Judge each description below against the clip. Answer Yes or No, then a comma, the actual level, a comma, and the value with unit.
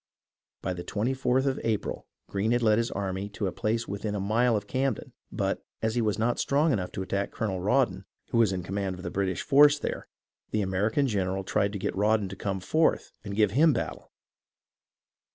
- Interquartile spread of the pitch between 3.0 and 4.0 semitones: Yes, average, 3.3 semitones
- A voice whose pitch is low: Yes, low, 105 Hz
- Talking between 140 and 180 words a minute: No, average, 200 wpm